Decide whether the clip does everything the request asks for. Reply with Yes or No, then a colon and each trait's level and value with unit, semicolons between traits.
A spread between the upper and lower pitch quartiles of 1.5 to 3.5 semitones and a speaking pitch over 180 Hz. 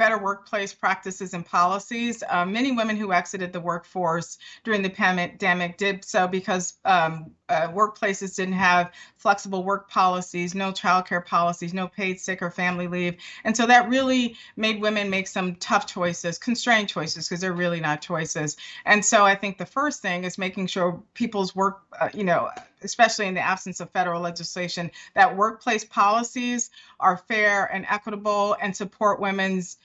Yes: average, 2.8 semitones; high, 190 Hz